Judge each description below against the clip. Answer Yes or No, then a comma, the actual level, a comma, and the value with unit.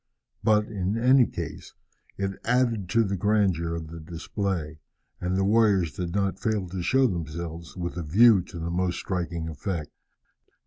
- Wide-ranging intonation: No, average, 3.8 semitones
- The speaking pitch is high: No, very low, 95 Hz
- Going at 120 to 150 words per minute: No, average, 165 wpm